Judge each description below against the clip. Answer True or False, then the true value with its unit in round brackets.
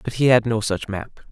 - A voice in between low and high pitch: False (110 Hz)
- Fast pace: True (275 wpm)